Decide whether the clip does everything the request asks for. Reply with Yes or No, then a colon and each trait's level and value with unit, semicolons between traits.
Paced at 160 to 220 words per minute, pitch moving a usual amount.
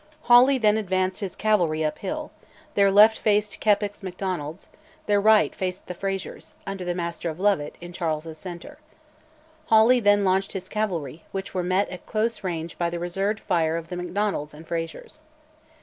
Yes: average, 170 wpm; average, 3.4 semitones